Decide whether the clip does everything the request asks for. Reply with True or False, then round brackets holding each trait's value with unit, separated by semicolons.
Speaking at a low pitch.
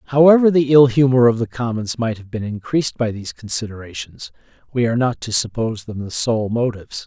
True (120 Hz)